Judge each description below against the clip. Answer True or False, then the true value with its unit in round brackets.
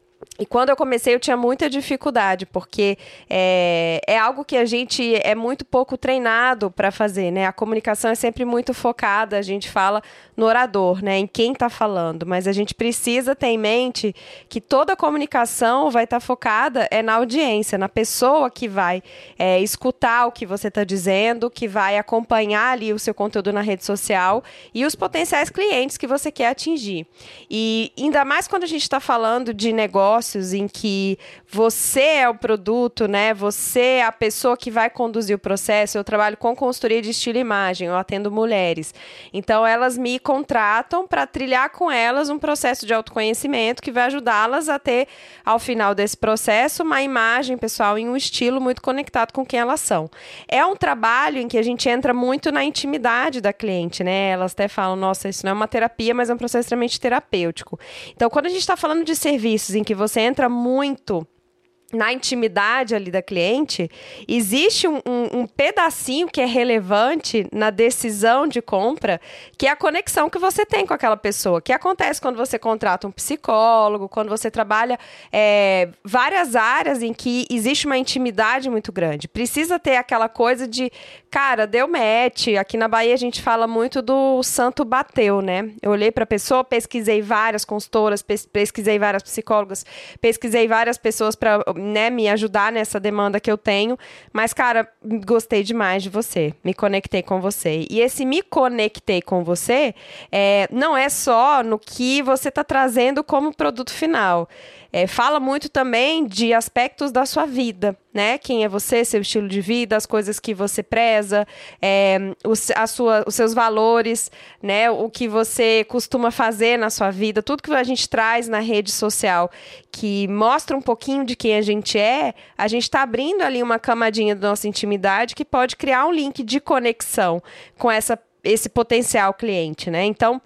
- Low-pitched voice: False (230 Hz)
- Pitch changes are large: False (3.5 semitones)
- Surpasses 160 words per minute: True (180 wpm)